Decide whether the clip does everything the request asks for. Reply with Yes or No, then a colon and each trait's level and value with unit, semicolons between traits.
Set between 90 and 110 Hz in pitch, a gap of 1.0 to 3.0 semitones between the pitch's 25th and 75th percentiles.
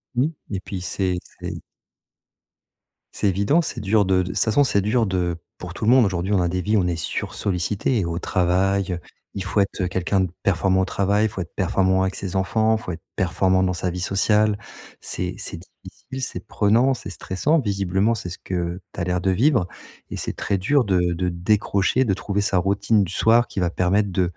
Yes: very low, 95 Hz; narrow, 2.6 semitones